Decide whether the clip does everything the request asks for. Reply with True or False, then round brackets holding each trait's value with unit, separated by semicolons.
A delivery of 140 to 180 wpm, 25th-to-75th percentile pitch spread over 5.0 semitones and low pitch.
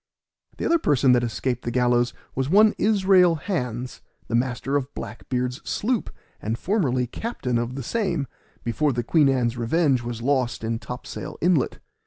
True (165 wpm; 5.6 semitones; 130 Hz)